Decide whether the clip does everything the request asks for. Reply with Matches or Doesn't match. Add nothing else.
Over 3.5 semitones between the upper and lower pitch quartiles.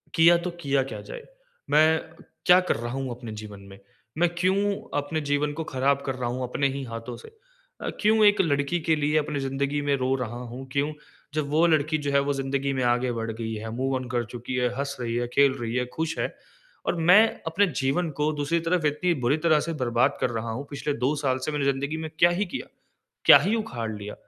Matches